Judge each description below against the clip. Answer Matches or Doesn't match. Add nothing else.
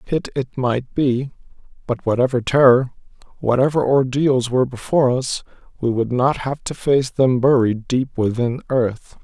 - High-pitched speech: Doesn't match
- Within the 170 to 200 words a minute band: Doesn't match